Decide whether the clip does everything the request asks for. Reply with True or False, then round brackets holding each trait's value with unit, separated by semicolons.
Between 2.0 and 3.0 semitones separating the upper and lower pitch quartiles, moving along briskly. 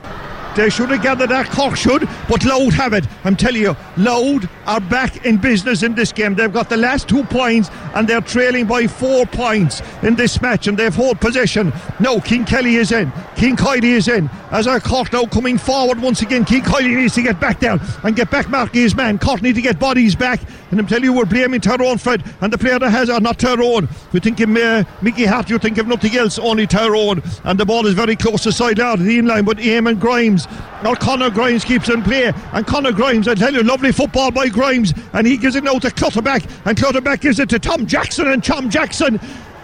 True (2.6 semitones; 230 wpm)